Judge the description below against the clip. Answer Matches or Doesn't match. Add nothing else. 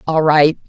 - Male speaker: Doesn't match